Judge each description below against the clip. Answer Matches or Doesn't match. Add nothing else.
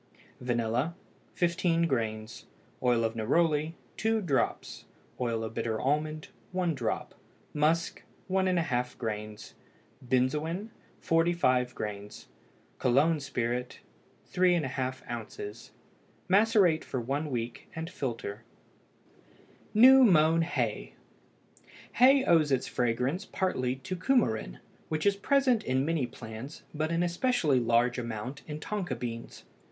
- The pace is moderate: Doesn't match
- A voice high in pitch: Doesn't match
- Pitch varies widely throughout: Matches